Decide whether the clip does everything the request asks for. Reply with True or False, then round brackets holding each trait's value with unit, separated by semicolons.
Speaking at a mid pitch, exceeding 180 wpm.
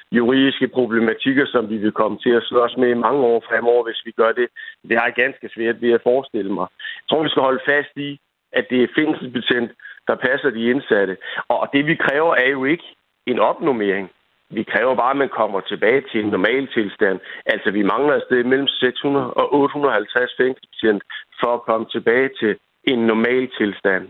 False (125 Hz; 195 wpm)